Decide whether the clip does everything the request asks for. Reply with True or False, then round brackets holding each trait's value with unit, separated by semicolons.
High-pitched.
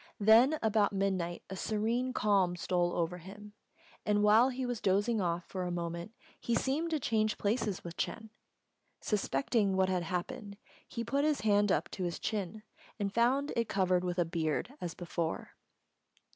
True (205 Hz)